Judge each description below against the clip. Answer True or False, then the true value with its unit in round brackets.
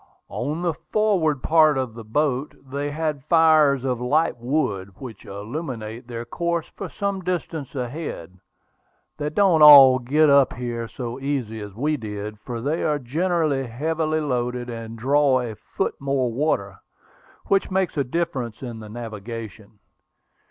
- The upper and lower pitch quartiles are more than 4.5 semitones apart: True (4.9 semitones)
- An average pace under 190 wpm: True (150 wpm)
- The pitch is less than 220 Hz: True (135 Hz)